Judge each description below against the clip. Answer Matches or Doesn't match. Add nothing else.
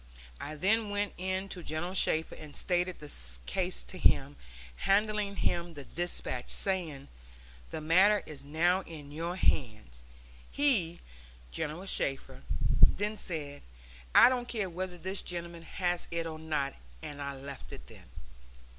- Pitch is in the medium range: Matches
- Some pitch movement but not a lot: Matches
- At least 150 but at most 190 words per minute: Doesn't match